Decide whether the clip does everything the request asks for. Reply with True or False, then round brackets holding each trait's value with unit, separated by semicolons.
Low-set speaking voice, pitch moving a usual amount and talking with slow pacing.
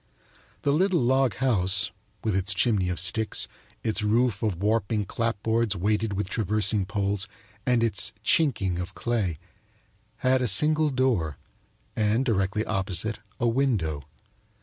True (110 Hz; 3.7 semitones; 130 wpm)